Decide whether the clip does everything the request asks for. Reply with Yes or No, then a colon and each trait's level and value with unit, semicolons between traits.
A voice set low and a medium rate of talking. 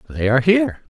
Yes: low, 125 Hz; average, 190 wpm